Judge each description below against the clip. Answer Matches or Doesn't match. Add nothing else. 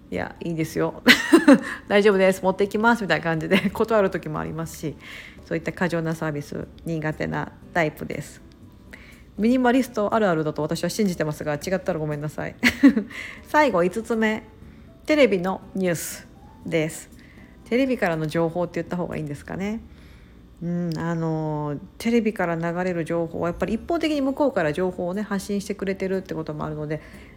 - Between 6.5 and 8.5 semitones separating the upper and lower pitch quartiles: Doesn't match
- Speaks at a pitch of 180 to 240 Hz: Matches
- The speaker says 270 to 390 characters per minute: Matches